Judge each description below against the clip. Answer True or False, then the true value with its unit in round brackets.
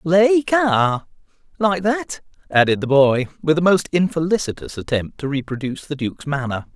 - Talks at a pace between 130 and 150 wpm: True (135 wpm)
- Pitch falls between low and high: True (160 Hz)